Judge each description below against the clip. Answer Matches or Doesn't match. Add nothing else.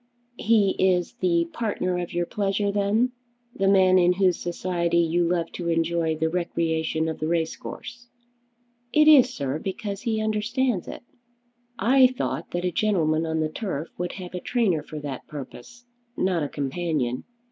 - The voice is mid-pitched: Matches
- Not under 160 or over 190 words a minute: Matches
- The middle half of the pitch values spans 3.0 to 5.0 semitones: Matches